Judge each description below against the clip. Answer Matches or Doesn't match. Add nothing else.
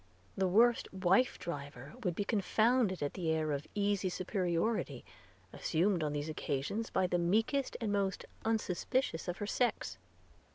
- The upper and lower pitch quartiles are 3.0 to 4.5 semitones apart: Doesn't match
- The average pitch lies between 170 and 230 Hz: Matches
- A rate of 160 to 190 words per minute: Doesn't match